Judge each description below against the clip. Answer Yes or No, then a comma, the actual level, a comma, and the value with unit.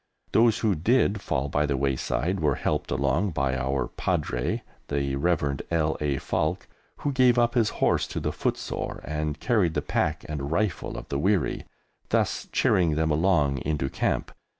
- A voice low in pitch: Yes, very low, 75 Hz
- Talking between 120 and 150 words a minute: No, average, 170 wpm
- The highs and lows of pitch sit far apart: Yes, wide, 5.9 semitones